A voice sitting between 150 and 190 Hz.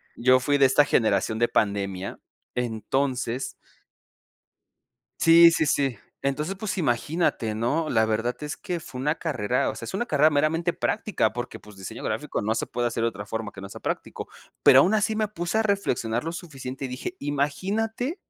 No: low, 135 Hz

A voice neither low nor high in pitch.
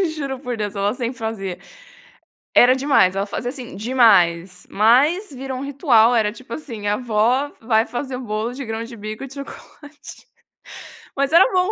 No: high, 240 Hz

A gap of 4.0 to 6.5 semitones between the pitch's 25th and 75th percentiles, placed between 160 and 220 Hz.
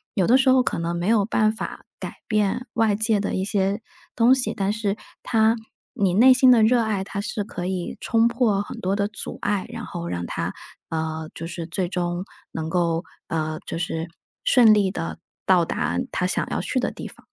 Yes: average, 4.4 semitones; high, 200 Hz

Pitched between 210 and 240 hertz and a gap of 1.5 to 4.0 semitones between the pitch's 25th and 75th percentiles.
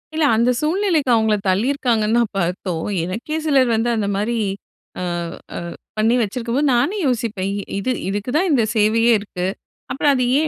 No: high, 230 Hz; average, 4.7 semitones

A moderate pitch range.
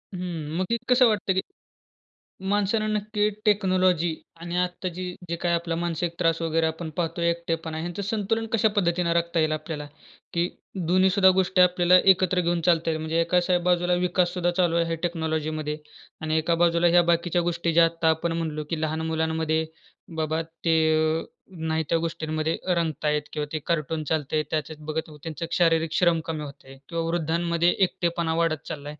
No: narrow, 1.9 semitones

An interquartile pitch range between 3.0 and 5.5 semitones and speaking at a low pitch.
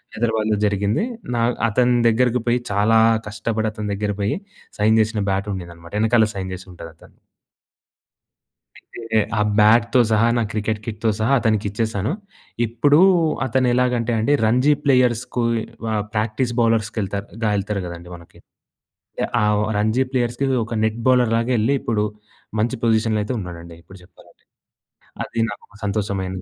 No: narrow, 2.4 semitones; low, 110 Hz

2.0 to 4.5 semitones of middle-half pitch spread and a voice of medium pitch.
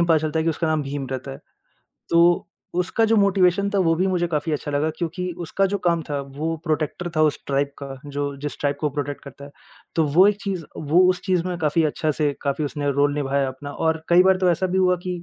Yes: average, 3.9 semitones; medium, 160 Hz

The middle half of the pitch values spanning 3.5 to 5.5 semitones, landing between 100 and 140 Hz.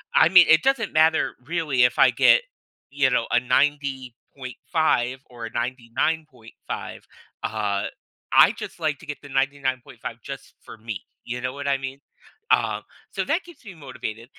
Yes: average, 4.3 semitones; low, 135 Hz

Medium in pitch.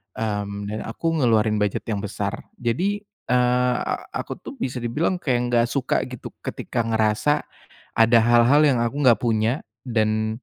No: low, 120 Hz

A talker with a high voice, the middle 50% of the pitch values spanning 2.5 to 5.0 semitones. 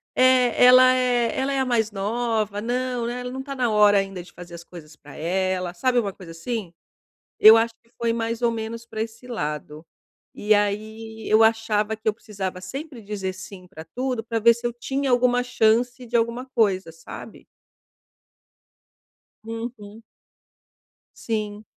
Yes: high, 225 Hz; average, 3.3 semitones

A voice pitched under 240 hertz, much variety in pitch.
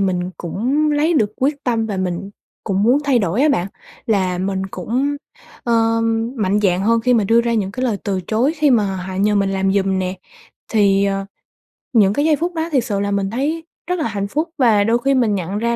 No: high, 215 Hz; average, 4.9 semitones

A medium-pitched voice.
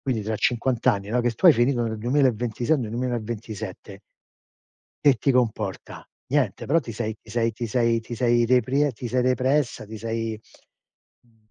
No: low, 120 Hz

